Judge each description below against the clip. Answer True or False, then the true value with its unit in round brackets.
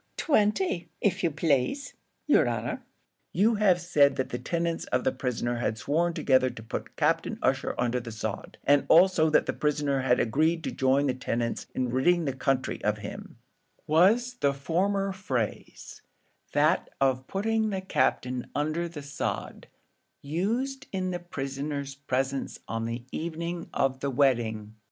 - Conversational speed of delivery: True (155 wpm)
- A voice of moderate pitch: True (145 Hz)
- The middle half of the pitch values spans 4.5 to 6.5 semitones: True (5.2 semitones)